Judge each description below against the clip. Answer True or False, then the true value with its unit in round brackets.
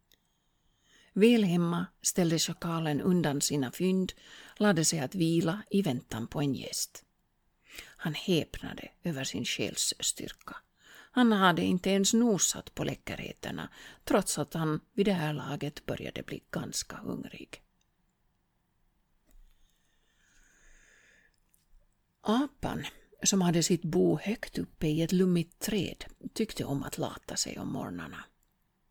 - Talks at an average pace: False (115 wpm)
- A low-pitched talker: False (175 Hz)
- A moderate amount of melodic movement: True (4.9 semitones)